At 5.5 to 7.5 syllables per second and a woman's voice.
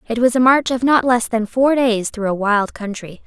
No: 4.9 syllables/s; female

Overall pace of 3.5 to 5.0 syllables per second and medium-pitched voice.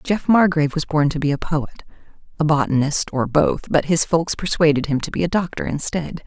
No: 5.4 syllables/s; medium, 155 Hz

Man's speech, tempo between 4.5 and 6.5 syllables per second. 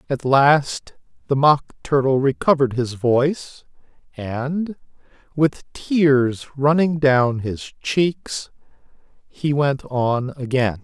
No: male; 3.2 syllables/s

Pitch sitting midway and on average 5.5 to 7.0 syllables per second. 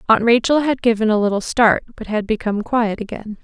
No: high, 225 Hz; 5.8 syllables/s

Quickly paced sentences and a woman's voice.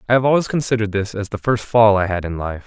No: fast, 290 wpm; male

